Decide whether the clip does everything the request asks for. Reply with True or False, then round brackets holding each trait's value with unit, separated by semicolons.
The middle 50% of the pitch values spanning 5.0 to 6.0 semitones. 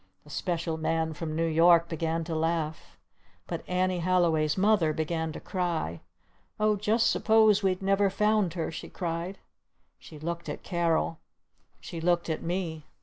False (2.5 semitones)